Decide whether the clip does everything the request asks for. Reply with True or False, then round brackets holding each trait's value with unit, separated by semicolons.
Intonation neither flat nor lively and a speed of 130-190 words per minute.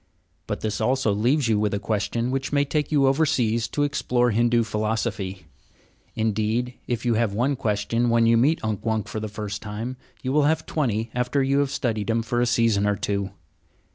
False (3.3 semitones; 200 wpm)